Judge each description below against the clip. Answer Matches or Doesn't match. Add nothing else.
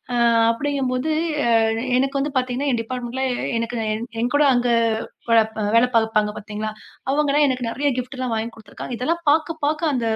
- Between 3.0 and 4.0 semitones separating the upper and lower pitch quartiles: Matches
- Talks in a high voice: Matches